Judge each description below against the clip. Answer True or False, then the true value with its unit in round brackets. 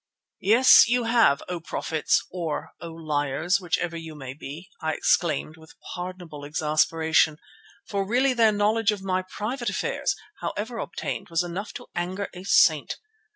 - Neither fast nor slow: True (150 wpm)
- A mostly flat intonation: False (4.6 semitones)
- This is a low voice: False (175 Hz)